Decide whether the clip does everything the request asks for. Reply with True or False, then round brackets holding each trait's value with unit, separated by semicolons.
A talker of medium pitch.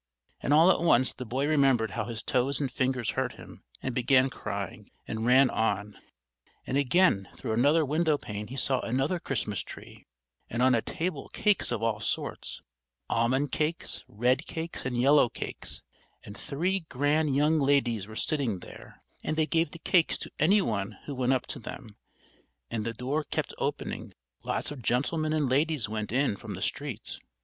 False (130 Hz)